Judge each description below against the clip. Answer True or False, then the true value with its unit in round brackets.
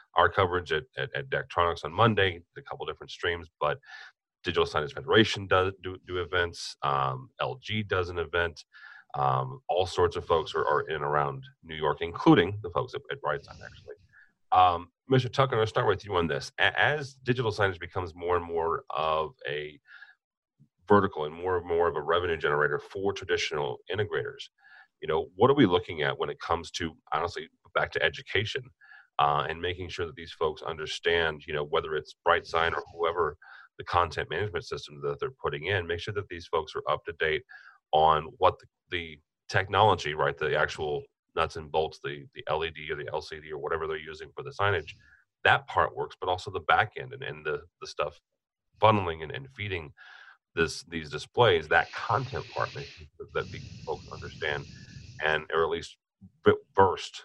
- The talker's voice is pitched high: True (395 Hz)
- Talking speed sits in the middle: True (190 wpm)